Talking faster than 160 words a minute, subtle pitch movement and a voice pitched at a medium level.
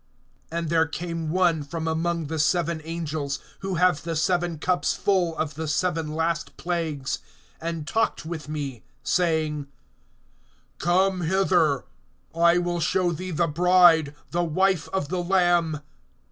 No: average, 140 wpm; narrow, 2.1 semitones; medium, 165 Hz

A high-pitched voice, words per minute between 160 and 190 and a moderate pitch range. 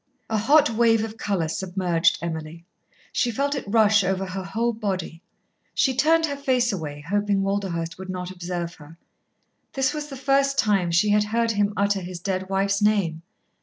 Yes: high, 200 Hz; average, 175 wpm; average, 4.2 semitones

